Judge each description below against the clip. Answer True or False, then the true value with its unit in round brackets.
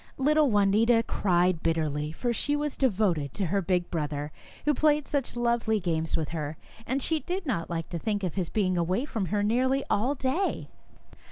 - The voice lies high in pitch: True (205 Hz)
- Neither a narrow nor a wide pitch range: False (7.5 semitones)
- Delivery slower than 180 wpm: False (185 wpm)